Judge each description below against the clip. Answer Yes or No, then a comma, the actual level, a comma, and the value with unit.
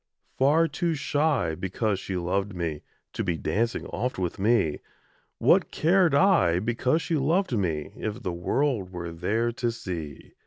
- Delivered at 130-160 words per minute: Yes, average, 155 wpm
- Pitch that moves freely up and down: Yes, wide, 8.0 semitones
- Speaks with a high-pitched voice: No, low, 105 Hz